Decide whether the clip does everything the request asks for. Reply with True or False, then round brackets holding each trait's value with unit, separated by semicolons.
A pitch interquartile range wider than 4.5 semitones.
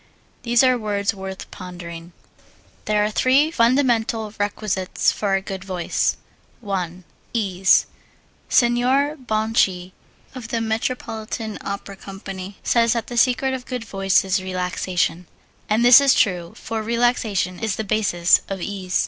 False (3.9 semitones)